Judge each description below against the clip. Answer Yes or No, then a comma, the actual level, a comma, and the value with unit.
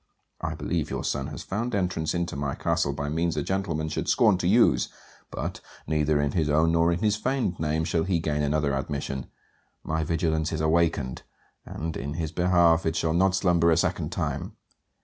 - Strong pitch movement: No, narrow, 2.6 semitones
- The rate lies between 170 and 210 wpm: Yes, average, 190 wpm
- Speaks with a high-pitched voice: No, very low, 80 Hz